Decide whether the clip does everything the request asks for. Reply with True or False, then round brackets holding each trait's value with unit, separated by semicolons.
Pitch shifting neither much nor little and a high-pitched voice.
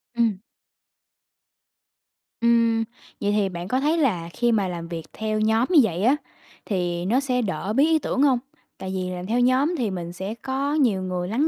False (5.7 semitones; 220 Hz)